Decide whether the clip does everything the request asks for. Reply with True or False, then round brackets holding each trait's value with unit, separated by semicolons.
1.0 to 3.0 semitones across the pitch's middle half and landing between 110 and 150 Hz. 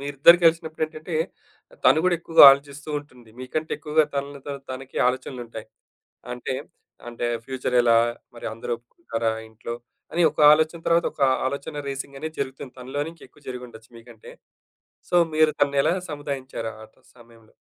False (4.0 semitones; 140 Hz)